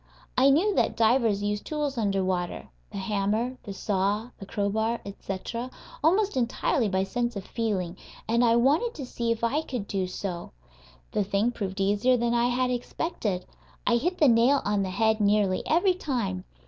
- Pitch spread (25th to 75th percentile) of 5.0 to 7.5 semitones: No, average, 4.1 semitones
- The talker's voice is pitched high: Yes, high, 225 Hz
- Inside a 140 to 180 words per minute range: Yes, average, 175 wpm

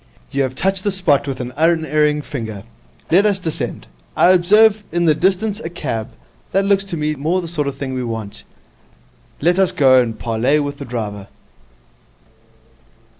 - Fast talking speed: No, average, 175 wpm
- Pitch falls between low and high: Yes, medium, 150 Hz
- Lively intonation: Yes, wide, 6.1 semitones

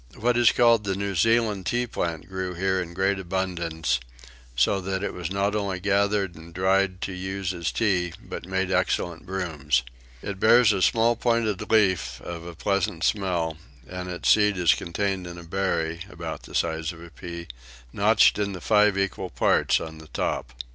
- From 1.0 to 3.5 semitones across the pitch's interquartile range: Yes, average, 2.9 semitones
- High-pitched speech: No, very low, 95 Hz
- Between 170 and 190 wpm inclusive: Yes, average, 180 wpm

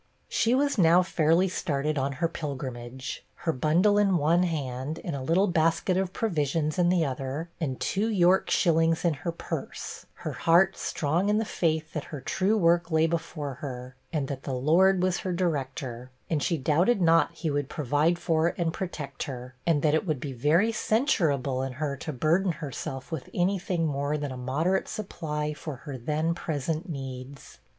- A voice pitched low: No, medium, 160 Hz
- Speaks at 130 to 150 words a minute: No, average, 185 wpm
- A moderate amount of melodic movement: Yes, average, 3.9 semitones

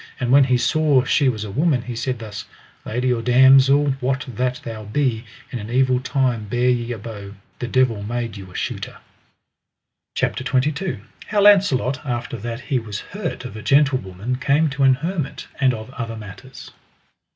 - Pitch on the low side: Yes, low, 125 Hz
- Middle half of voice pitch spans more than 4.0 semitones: No, average, 3.0 semitones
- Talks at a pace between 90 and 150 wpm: No, average, 180 wpm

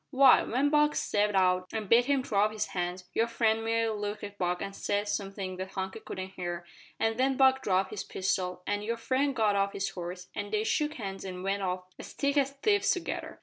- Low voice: No, high, 205 Hz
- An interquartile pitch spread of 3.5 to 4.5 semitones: Yes, average, 4.1 semitones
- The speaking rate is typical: No, fast, 225 wpm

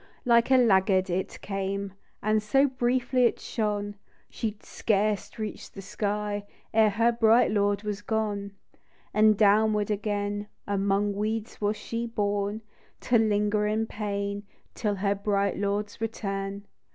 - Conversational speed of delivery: Yes, average, 150 wpm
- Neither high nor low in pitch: No, high, 210 Hz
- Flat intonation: Yes, narrow, 1.4 semitones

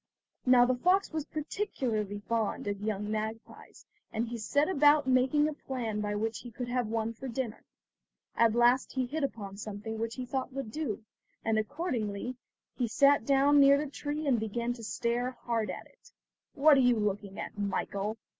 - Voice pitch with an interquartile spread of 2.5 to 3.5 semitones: No, average, 4.0 semitones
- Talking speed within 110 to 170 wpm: No, average, 185 wpm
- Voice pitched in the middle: No, high, 240 Hz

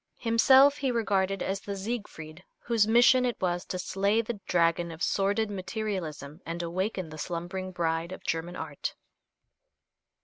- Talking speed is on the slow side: No, average, 145 wpm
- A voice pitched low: No, high, 190 Hz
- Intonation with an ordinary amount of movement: Yes, average, 4.4 semitones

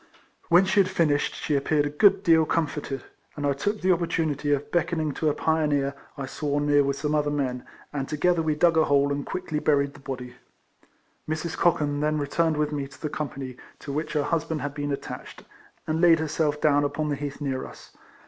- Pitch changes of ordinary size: No, narrow, 2.0 semitones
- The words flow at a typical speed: No, fast, 210 wpm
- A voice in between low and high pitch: Yes, medium, 150 Hz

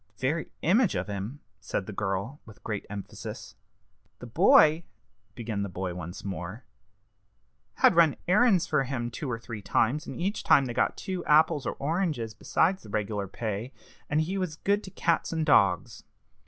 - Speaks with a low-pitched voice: Yes, low, 130 Hz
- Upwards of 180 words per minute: No, average, 175 wpm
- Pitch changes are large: Yes, wide, 8.0 semitones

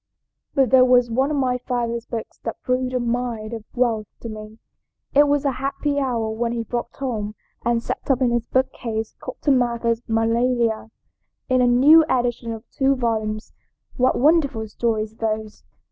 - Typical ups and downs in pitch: No, narrow, 2.3 semitones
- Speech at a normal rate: Yes, average, 170 wpm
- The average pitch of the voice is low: No, high, 240 Hz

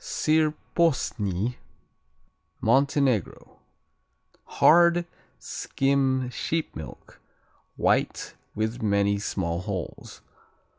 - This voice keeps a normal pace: No, slow, 65 wpm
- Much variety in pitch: Yes, wide, 6.9 semitones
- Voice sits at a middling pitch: No, low, 125 Hz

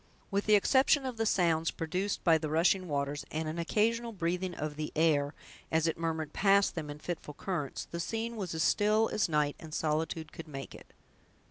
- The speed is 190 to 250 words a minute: Yes, average, 200 wpm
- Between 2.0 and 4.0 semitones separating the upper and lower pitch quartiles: No, average, 4.4 semitones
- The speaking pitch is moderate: Yes, medium, 165 Hz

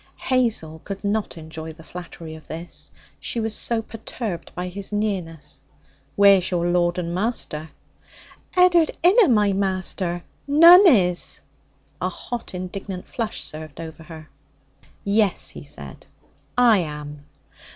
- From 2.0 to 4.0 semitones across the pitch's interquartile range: No, average, 5.1 semitones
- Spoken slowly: Yes, slow, 130 wpm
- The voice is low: No, medium, 185 Hz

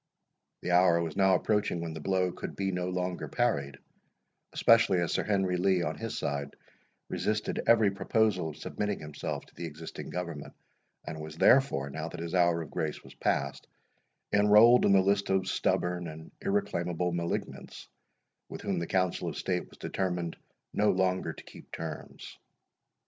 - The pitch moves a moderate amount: Yes, average, 3.1 semitones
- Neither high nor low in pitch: No, very low, 90 Hz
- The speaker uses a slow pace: No, average, 165 wpm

